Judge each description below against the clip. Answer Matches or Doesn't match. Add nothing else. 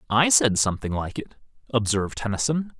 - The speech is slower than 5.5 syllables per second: Doesn't match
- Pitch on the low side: Matches